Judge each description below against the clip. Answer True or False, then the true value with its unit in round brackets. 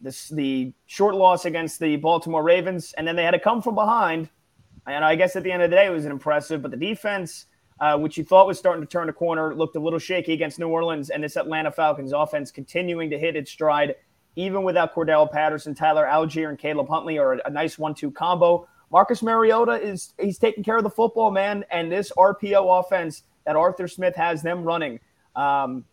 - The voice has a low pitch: False (165 Hz)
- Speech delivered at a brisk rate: True (220 wpm)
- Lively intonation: False (3.3 semitones)